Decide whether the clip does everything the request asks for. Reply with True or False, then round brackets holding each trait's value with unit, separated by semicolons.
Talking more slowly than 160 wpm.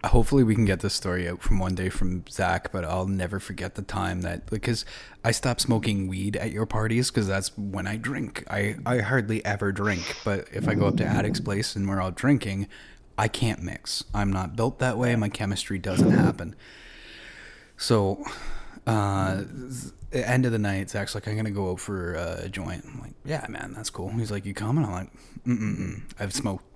False (205 wpm)